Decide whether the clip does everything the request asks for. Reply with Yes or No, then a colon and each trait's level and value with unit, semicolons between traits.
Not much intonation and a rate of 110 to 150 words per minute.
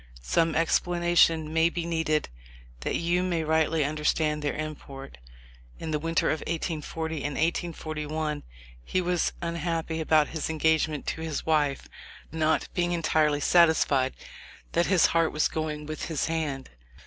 Yes: narrow, 1.5 semitones; average, 145 wpm